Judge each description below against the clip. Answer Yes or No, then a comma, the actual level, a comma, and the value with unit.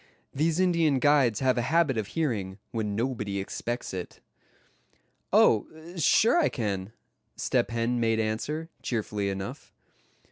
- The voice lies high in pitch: No, low, 120 Hz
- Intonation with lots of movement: Yes, wide, 6.1 semitones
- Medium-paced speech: No, slow, 130 wpm